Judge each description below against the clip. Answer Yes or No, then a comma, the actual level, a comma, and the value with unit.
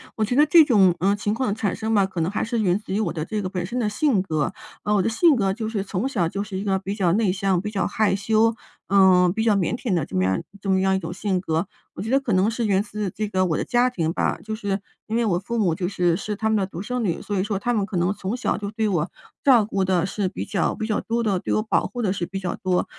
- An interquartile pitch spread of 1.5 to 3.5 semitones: Yes, average, 2.9 semitones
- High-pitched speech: Yes, high, 200 Hz